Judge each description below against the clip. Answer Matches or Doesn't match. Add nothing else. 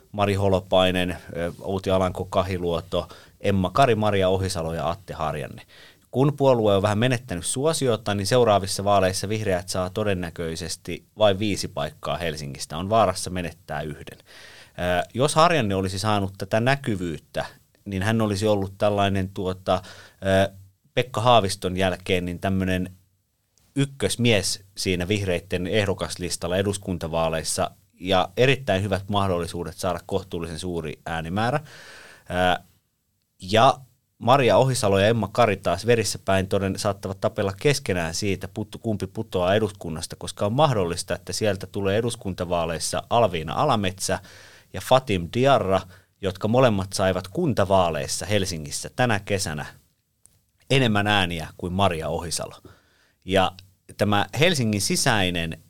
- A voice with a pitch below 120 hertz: Matches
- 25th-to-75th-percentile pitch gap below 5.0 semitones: Matches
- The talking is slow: Doesn't match